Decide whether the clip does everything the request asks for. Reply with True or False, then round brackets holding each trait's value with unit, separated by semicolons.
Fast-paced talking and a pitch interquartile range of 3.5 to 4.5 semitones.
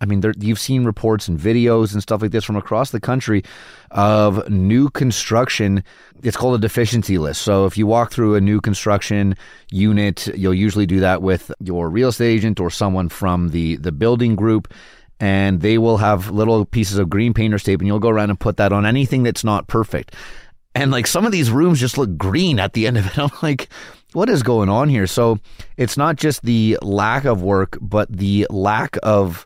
False (210 wpm; 3.0 semitones)